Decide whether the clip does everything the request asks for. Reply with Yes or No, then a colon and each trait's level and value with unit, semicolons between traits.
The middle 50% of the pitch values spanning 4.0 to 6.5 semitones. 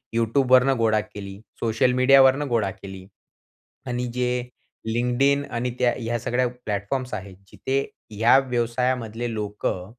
No: average, 2.8 semitones